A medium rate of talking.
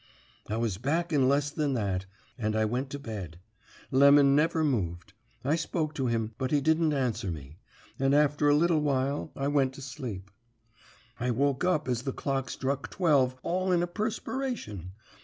Yes: average, 175 wpm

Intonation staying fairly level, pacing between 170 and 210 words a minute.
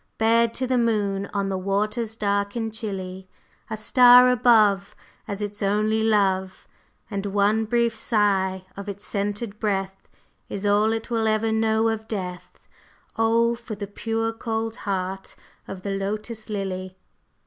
No: narrow, 2.2 semitones; average, 150 wpm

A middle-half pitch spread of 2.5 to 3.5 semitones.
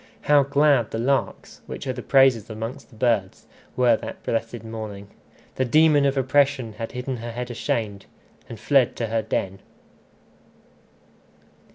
Yes: average, 3.1 semitones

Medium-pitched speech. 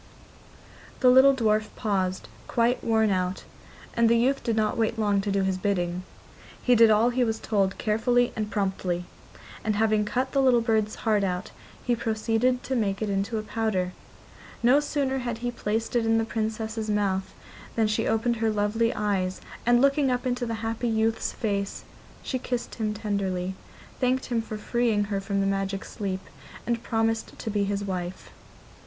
No: high, 220 Hz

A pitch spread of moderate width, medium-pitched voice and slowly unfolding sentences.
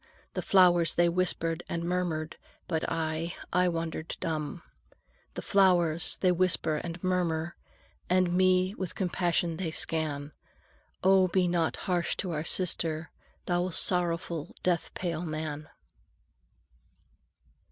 No: narrow, 2.1 semitones; medium, 170 Hz; slow, 120 wpm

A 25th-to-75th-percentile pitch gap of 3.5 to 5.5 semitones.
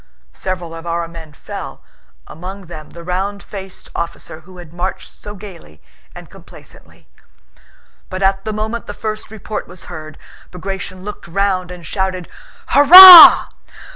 No: average, 2.9 semitones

